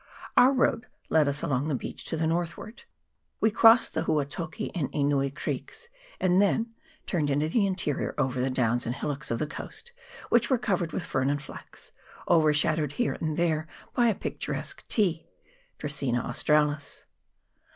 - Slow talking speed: No, average, 165 wpm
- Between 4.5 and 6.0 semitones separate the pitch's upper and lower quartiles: Yes, average, 5.2 semitones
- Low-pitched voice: No, medium, 155 Hz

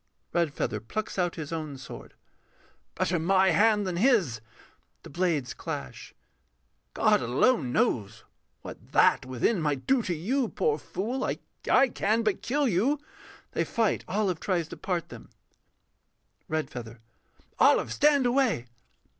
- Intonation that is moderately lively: No, wide, 7.7 semitones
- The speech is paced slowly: Yes, slow, 130 wpm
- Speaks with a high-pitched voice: No, medium, 180 Hz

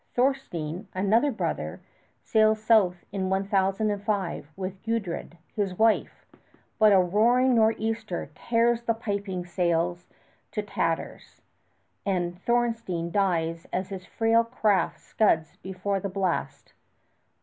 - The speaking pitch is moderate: No, high, 200 Hz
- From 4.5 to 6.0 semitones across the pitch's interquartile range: No, average, 3.7 semitones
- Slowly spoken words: Yes, slow, 110 wpm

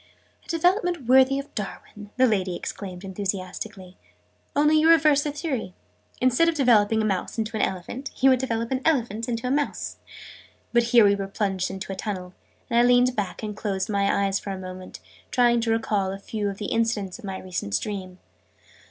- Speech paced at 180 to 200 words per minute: Yes, average, 190 wpm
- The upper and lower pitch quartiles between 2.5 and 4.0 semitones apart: No, average, 4.8 semitones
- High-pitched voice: Yes, high, 220 Hz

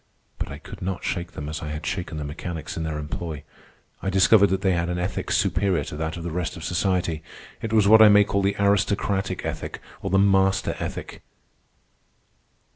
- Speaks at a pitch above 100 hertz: No, very low, 90 Hz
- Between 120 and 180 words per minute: No, average, 200 wpm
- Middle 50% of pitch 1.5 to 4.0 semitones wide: Yes, average, 3.4 semitones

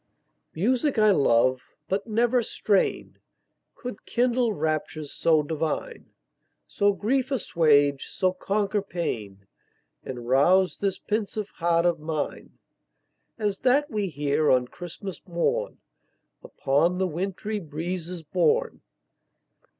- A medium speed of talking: No, slow, 110 wpm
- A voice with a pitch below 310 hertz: Yes, medium, 185 Hz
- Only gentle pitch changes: No, wide, 5.6 semitones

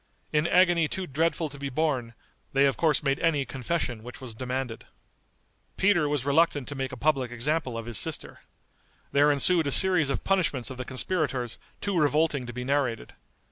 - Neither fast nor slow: Yes, average, 180 wpm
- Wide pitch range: No, average, 4.0 semitones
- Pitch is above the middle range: No, medium, 140 Hz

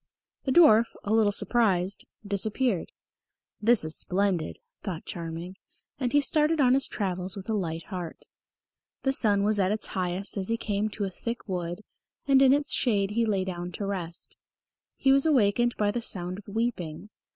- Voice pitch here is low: No, high, 205 Hz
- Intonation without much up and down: No, average, 4.2 semitones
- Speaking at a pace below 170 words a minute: No, average, 175 wpm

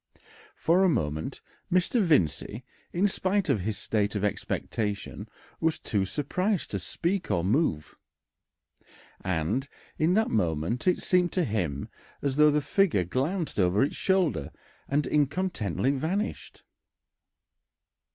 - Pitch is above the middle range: No, medium, 140 Hz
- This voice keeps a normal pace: No, slow, 125 wpm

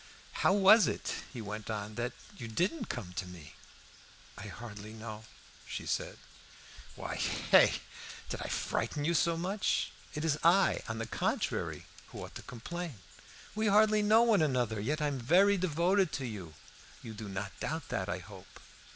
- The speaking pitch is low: Yes, low, 130 Hz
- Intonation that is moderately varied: No, wide, 9.0 semitones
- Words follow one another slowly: No, average, 170 wpm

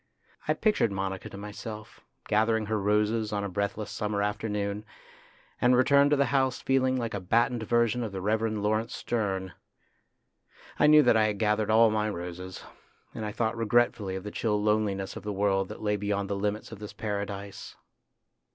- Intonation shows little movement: Yes, narrow, 2.0 semitones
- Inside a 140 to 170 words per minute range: No, average, 180 wpm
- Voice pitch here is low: Yes, low, 105 Hz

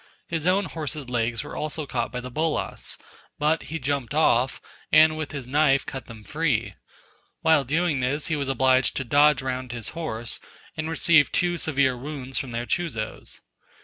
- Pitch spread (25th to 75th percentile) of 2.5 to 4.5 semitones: Yes, average, 3.7 semitones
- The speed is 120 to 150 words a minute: No, average, 175 wpm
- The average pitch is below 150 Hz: Yes, medium, 140 Hz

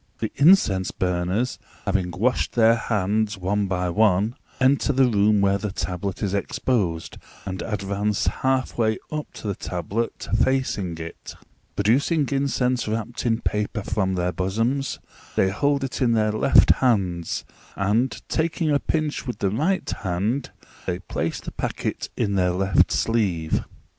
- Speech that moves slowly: No, average, 150 wpm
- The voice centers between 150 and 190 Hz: No, low, 105 Hz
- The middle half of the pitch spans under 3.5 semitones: No, average, 4.9 semitones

